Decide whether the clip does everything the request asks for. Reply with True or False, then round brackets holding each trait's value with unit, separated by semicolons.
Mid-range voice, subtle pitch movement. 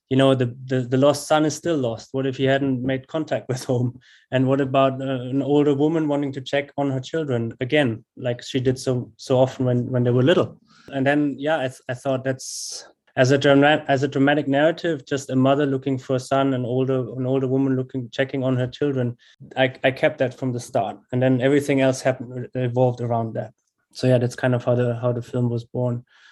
False (130 Hz; 1.7 semitones)